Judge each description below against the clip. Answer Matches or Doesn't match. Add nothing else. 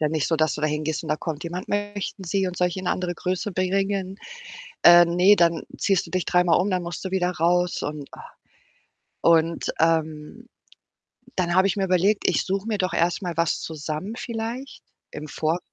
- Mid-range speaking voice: Matches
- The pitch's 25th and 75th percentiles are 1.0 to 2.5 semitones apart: Doesn't match